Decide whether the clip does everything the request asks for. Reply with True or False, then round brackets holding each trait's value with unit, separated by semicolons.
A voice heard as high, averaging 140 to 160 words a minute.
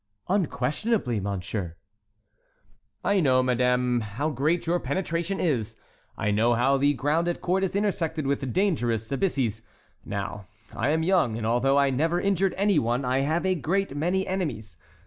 False (140 Hz; 155 wpm)